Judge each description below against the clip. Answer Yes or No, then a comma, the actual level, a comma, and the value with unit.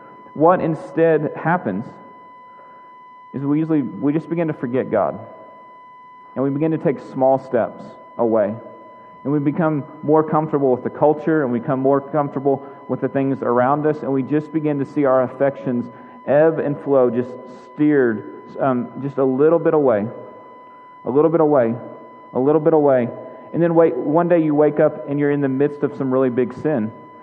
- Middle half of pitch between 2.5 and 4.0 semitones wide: Yes, average, 3.3 semitones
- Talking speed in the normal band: Yes, average, 185 wpm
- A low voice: No, medium, 145 Hz